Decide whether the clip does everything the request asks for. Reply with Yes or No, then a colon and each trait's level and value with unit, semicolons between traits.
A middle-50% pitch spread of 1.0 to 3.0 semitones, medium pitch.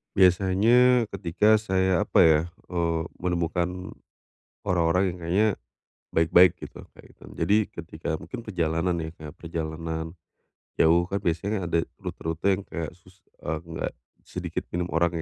No: narrow, 2.5 semitones; very low, 85 Hz